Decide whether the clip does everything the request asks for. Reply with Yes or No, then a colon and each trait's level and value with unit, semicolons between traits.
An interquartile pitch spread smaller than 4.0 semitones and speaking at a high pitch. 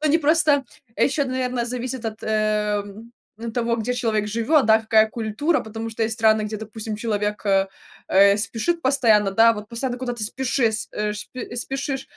Yes: average, 3.1 semitones; high, 225 Hz